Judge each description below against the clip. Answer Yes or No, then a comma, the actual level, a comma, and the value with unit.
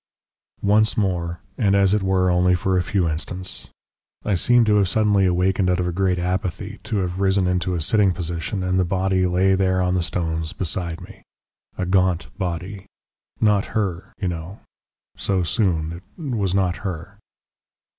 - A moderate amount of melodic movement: No, narrow, 1.9 semitones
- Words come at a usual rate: Yes, average, 175 wpm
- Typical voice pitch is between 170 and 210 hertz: No, very low, 95 Hz